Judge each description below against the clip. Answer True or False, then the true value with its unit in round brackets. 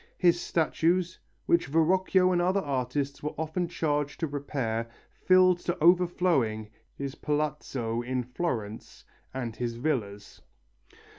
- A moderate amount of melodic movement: False (5.8 semitones)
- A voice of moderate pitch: True (150 Hz)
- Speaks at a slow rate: True (120 wpm)